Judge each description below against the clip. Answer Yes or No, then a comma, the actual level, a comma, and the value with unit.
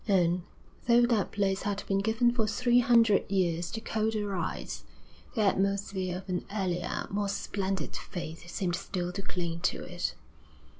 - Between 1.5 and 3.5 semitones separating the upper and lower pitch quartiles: Yes, average, 3.2 semitones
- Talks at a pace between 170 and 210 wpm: No, average, 155 wpm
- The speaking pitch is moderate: No, high, 195 Hz